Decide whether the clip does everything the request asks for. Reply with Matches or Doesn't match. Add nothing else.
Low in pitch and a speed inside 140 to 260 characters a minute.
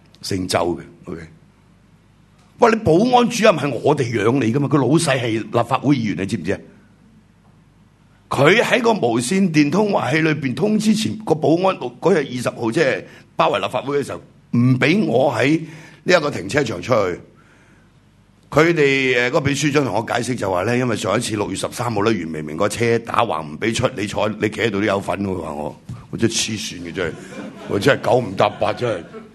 Doesn't match